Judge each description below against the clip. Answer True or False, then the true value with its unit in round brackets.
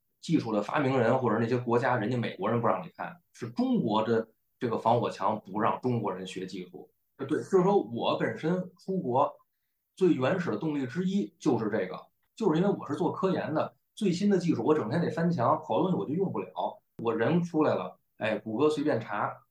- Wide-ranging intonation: True (7.2 semitones)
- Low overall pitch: True (130 Hz)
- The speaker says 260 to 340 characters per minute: True (310 characters per minute)